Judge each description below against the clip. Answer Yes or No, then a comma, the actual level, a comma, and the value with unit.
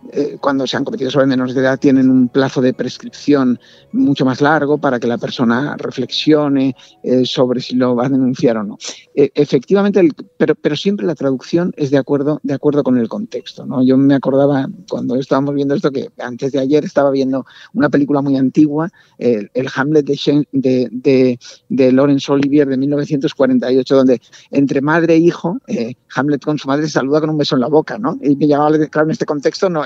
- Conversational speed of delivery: No, fast, 200 wpm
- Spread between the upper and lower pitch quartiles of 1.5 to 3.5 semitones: Yes, narrow, 2.4 semitones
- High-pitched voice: No, medium, 140 Hz